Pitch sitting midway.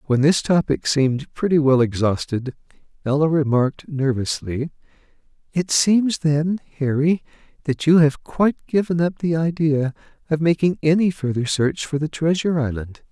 Yes: medium, 150 Hz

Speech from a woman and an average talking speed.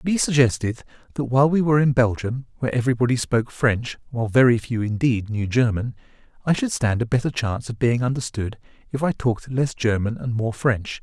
No: male; average, 190 wpm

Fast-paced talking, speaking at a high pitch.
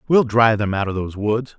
No: fast, 265 wpm; low, 110 Hz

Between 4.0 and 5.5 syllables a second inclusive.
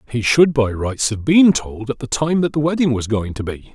Yes: 5.1 syllables/s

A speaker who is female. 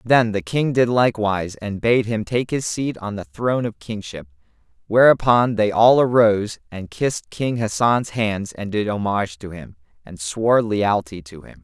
No: male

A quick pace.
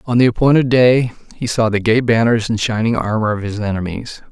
Yes: fast, 210 wpm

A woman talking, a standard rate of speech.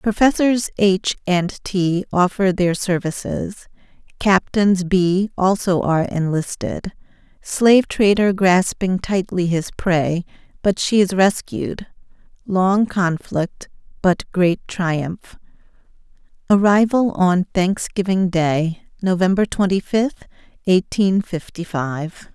No: female; slow, 90 wpm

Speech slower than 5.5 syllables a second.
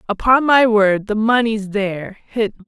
Yes: 4.6 syllables/s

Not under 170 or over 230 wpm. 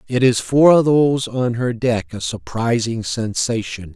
No: average, 150 wpm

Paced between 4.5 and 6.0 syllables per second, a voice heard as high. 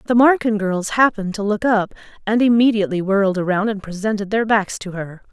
Yes: 5.9 syllables/s; high, 210 Hz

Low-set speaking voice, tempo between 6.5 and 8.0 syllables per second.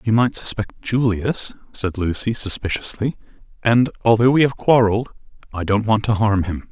No: low, 110 Hz; 5.0 syllables/s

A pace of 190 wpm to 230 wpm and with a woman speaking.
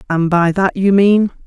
Yes: fast, 205 wpm; female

